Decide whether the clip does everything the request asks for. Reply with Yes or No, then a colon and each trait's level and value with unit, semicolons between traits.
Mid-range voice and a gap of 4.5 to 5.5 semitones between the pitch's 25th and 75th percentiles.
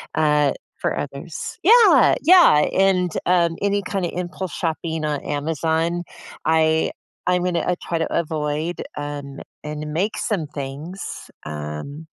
No: medium, 160 Hz; average, 3.3 semitones